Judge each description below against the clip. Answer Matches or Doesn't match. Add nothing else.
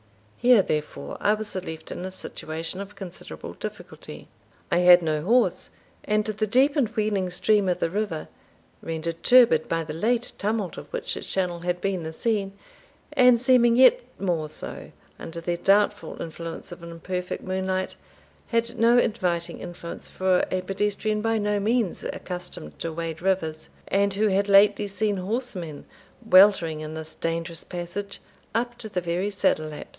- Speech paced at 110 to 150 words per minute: Doesn't match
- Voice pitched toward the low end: Doesn't match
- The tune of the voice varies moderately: Matches